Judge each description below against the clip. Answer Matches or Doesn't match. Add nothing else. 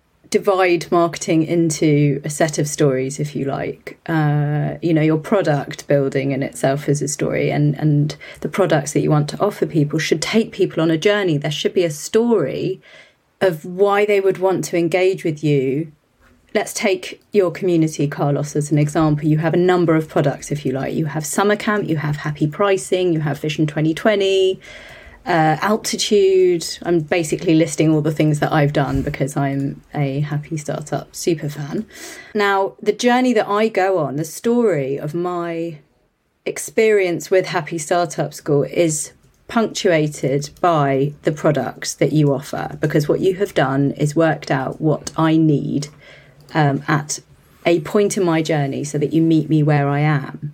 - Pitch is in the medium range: Matches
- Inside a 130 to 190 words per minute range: Matches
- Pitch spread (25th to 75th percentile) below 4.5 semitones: Matches